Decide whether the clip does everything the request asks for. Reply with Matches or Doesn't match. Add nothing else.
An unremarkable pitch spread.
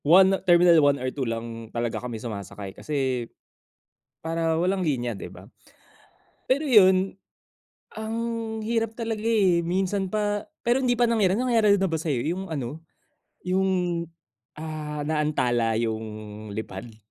Doesn't match